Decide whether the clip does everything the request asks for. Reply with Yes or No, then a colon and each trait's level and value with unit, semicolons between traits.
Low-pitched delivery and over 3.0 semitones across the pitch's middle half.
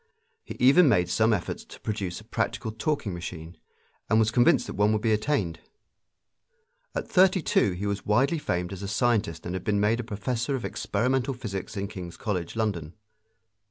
Yes: low, 105 Hz; average, 4.6 semitones